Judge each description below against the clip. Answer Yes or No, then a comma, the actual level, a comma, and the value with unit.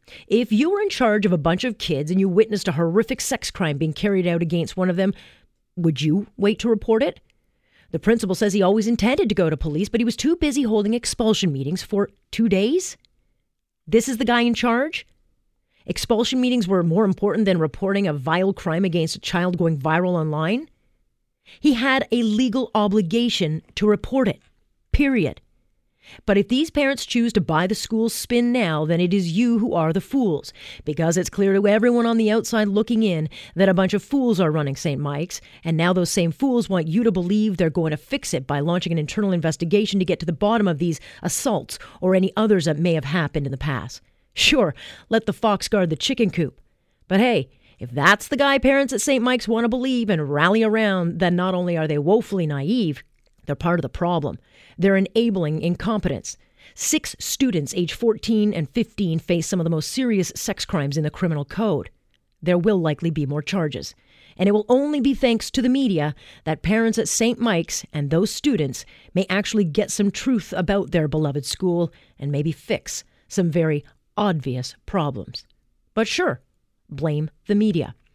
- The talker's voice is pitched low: No, high, 195 Hz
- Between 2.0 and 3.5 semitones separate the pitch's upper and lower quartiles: No, wide, 5.6 semitones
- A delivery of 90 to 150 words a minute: No, average, 200 wpm